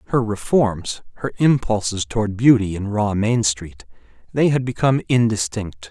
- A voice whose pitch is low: Yes, low, 110 Hz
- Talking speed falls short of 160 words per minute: Yes, average, 140 wpm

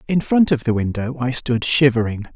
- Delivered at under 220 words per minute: Yes, fast, 205 wpm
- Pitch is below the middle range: Yes, low, 130 Hz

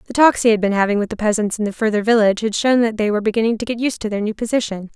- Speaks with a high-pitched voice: Yes, high, 220 Hz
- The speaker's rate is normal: No, fast, 315 wpm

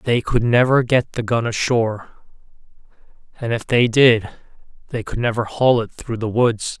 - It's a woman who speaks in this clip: No, male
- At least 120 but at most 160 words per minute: No, average, 170 wpm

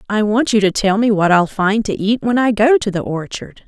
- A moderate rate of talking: No, fast, 280 wpm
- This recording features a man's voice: No, female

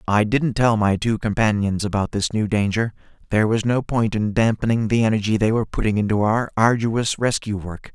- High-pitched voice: No, low, 110 Hz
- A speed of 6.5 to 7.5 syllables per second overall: No, 5.4 syllables/s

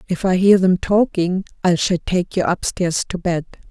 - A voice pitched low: No, medium, 185 Hz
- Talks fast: No, average, 195 wpm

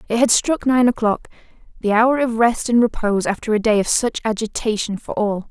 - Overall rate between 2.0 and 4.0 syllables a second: No, 5.5 syllables/s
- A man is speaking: No, female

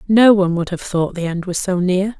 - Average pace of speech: No, fast, 275 wpm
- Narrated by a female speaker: Yes, female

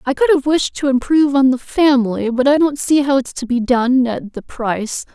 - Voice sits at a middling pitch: No, very high, 265 Hz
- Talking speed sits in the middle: No, fast, 245 wpm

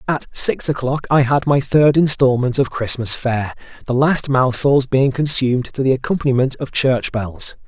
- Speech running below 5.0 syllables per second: Yes, 4.7 syllables/s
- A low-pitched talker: Yes, low, 130 Hz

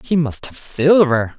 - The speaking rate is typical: Yes, average, 175 wpm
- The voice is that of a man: Yes, male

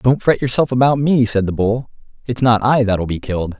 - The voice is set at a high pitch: No, low, 115 Hz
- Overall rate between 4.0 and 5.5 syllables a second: Yes, 5.3 syllables/s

